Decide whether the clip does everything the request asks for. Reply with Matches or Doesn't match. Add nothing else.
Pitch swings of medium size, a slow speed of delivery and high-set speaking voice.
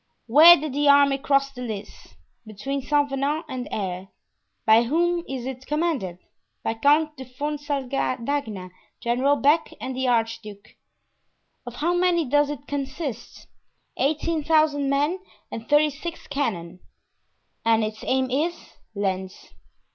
Matches